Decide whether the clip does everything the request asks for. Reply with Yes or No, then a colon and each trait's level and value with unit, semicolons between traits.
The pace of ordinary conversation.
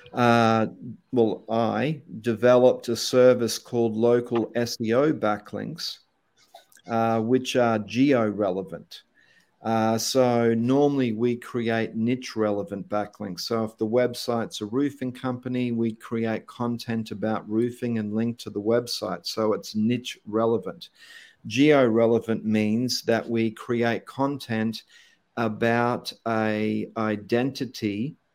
No: slow, 115 wpm